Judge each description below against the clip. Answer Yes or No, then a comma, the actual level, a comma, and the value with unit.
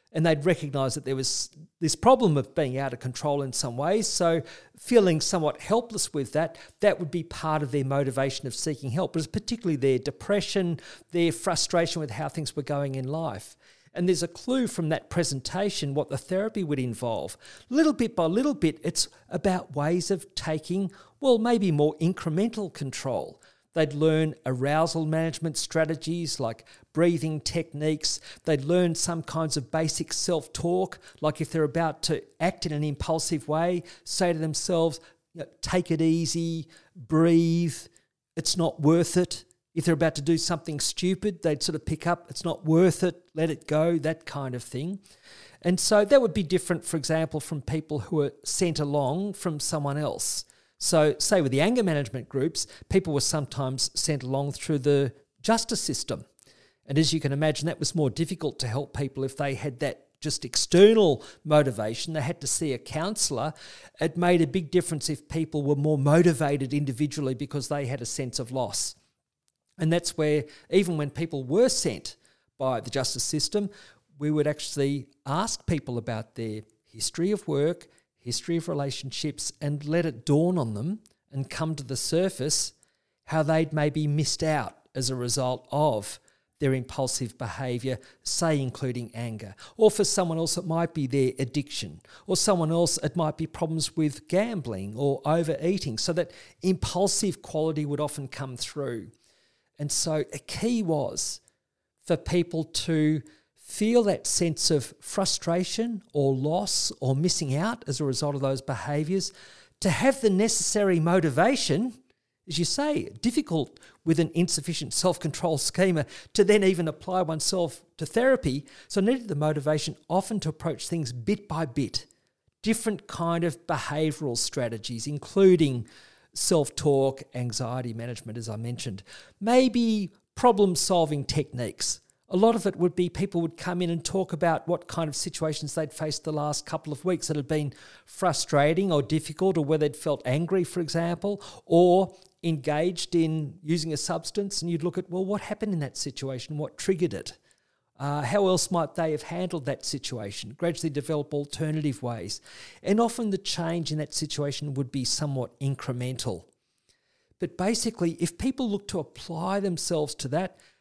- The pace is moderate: Yes, average, 170 wpm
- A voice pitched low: No, medium, 160 Hz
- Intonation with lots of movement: No, average, 3.8 semitones